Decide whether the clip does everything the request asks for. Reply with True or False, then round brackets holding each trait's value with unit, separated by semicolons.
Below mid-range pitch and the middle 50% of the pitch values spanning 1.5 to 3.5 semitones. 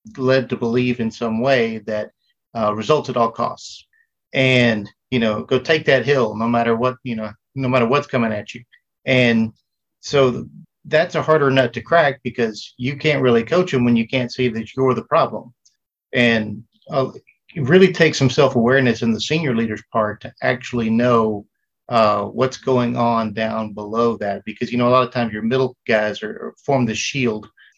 True (120 Hz; 2.8 semitones)